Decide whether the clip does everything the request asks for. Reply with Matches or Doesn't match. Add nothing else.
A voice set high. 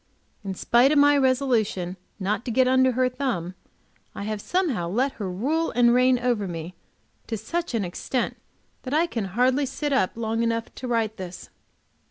Matches